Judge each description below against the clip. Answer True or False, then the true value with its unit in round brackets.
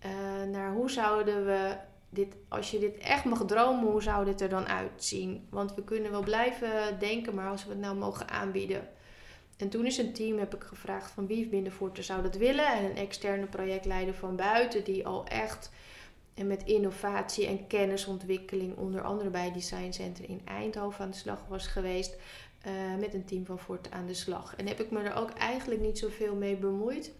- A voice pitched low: False (200 Hz)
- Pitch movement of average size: False (1.9 semitones)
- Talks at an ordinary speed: False (205 wpm)